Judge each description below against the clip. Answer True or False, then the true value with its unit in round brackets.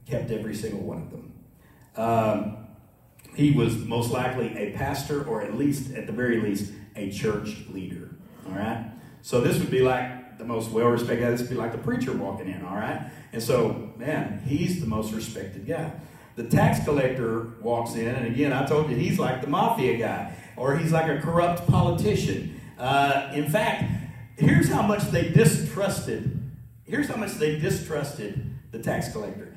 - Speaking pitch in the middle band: False (130 Hz)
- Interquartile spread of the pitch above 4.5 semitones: True (4.9 semitones)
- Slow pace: False (180 wpm)